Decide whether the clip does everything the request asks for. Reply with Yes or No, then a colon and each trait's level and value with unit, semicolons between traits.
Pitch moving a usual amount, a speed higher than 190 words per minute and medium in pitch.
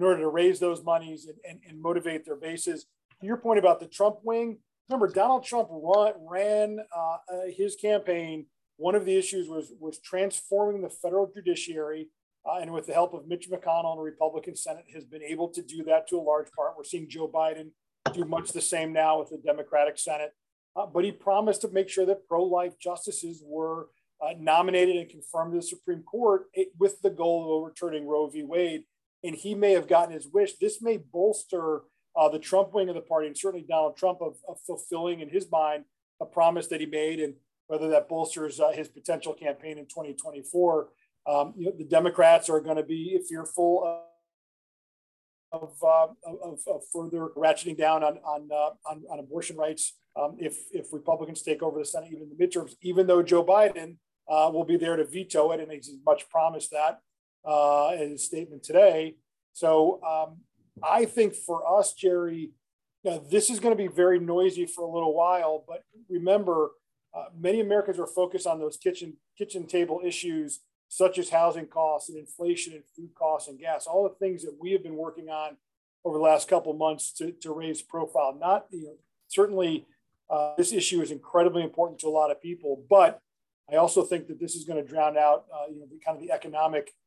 Yes: average, 3.0 semitones; average, 200 wpm; medium, 165 Hz